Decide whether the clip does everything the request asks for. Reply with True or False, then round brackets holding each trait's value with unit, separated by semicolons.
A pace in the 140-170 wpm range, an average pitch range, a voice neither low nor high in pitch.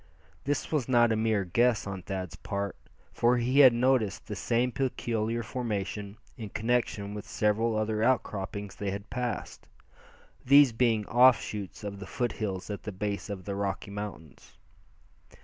False (155 wpm; 3.2 semitones; 110 Hz)